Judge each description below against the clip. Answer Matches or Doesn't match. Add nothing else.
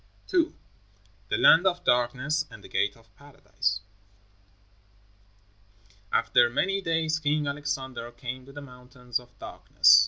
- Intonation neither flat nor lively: Matches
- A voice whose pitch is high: Doesn't match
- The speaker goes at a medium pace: Doesn't match